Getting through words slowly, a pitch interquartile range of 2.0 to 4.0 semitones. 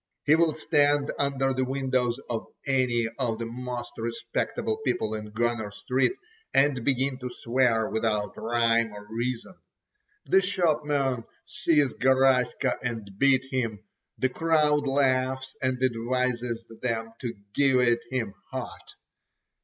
Yes: slow, 125 wpm; average, 2.7 semitones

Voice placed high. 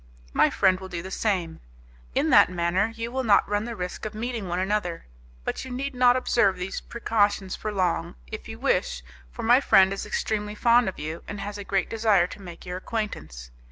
Yes: high, 200 Hz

